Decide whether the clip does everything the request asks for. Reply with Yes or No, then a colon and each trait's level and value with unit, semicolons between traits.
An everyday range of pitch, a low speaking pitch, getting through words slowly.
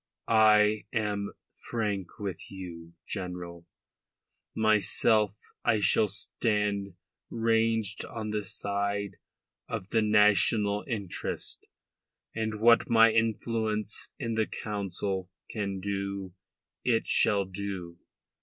No: narrow, 2.0 semitones; low, 105 Hz; slow, 100 wpm